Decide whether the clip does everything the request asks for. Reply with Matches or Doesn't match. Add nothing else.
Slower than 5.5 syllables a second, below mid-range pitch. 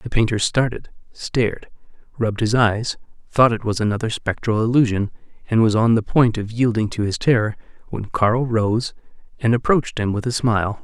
Matches